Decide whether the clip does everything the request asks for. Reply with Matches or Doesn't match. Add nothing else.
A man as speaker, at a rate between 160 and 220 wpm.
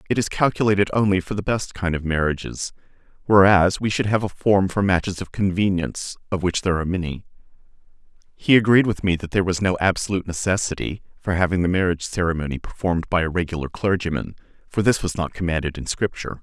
Matches